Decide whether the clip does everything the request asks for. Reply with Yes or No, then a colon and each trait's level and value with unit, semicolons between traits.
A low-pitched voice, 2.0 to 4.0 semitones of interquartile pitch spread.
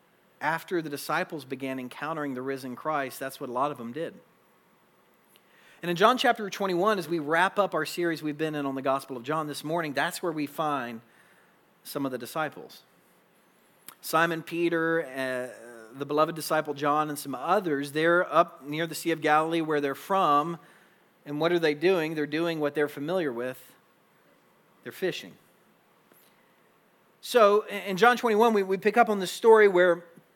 No: medium, 155 Hz; average, 3.5 semitones